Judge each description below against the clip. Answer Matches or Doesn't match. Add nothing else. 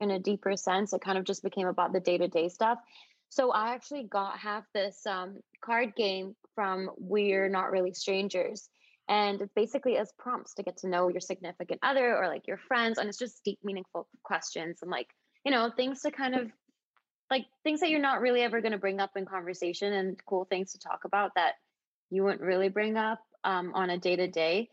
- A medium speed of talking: Doesn't match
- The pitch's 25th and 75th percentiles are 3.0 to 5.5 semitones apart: Matches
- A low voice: Doesn't match